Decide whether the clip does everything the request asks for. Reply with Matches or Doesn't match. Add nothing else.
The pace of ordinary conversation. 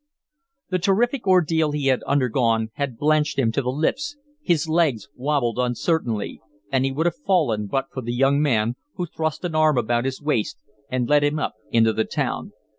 Matches